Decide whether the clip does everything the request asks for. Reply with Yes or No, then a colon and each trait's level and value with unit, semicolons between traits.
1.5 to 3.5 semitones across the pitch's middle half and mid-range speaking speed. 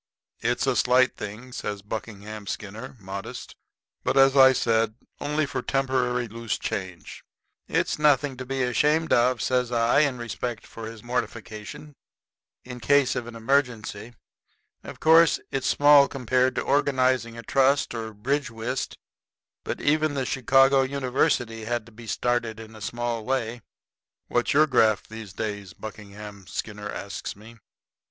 Yes: average, 3.2 semitones; average, 145 wpm